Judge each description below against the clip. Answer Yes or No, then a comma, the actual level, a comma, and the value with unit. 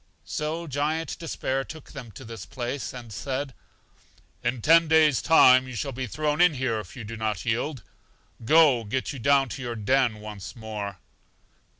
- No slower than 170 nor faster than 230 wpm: Yes, average, 175 wpm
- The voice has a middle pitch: No, low, 130 Hz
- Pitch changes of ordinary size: Yes, average, 4.7 semitones